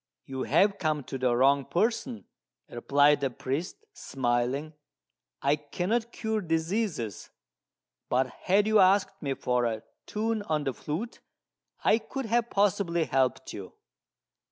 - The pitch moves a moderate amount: No, wide, 7.6 semitones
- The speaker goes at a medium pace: No, slow, 130 wpm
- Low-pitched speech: No, medium, 155 Hz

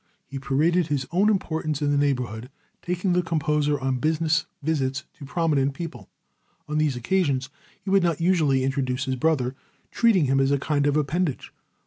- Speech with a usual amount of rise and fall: Yes, average, 3.6 semitones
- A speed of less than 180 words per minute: Yes, average, 170 wpm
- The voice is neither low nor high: Yes, medium, 150 Hz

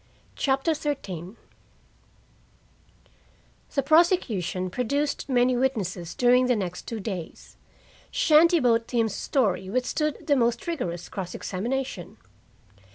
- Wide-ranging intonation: Yes, wide, 6.7 semitones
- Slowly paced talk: Yes, slow, 100 wpm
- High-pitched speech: Yes, high, 245 Hz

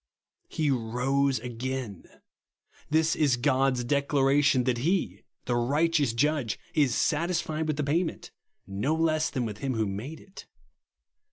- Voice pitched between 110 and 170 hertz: Yes, low, 135 Hz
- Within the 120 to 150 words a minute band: Yes, average, 140 wpm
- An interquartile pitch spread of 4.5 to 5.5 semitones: No, average, 4.0 semitones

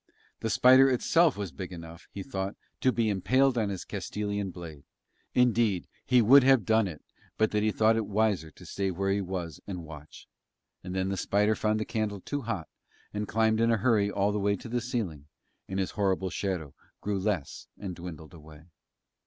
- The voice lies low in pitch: Yes, low, 100 Hz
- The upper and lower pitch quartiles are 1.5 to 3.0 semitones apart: No, average, 3.4 semitones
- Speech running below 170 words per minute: No, average, 195 wpm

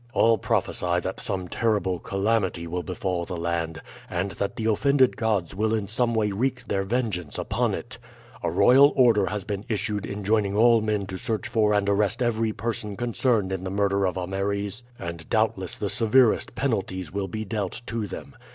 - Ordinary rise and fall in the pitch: Yes, average, 3.0 semitones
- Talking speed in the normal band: Yes, average, 180 wpm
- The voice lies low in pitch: Yes, low, 105 Hz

